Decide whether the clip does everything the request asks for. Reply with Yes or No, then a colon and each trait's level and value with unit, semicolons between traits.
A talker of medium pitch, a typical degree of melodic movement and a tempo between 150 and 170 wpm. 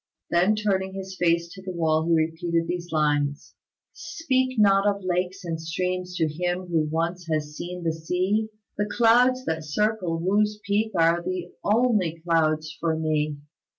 Yes: medium, 180 Hz; average, 3.7 semitones; average, 160 wpm